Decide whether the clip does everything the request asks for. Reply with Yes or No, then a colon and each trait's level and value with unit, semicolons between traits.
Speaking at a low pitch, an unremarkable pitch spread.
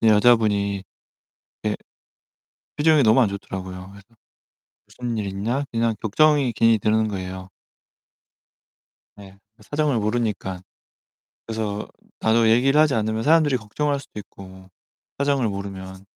Yes: low, 110 Hz; average, 4.0 semitones